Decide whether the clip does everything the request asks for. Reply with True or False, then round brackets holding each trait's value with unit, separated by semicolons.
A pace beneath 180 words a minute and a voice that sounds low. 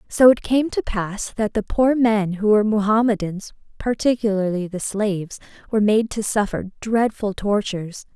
False (155 wpm; 210 Hz)